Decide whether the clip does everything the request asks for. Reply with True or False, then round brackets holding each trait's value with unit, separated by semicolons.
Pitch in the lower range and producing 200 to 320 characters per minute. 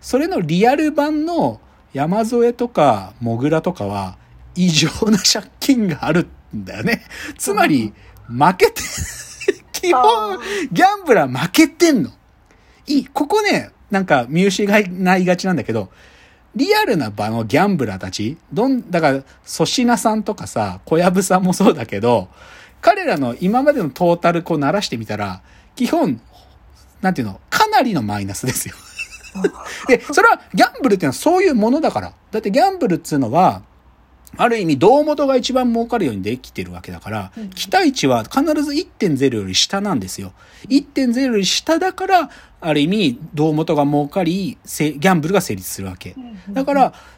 False (190 Hz; 315 characters per minute)